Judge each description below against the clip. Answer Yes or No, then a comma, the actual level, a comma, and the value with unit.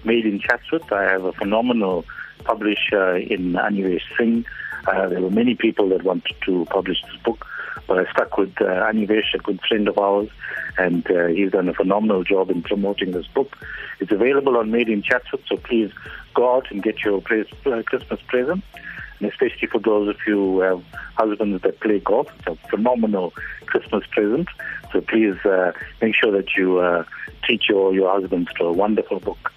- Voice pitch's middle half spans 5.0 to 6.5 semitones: No, average, 3.3 semitones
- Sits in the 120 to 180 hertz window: No, low, 105 Hz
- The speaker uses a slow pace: No, average, 185 wpm